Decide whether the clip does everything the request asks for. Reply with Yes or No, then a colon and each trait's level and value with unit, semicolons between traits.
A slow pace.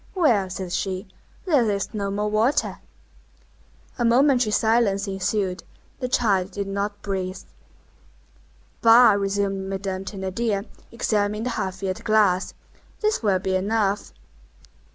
Yes: slow, 120 wpm